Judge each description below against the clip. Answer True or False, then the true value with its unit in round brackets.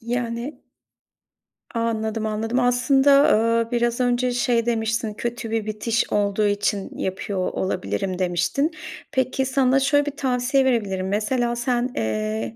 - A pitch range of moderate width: True (3.3 semitones)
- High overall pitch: True (235 Hz)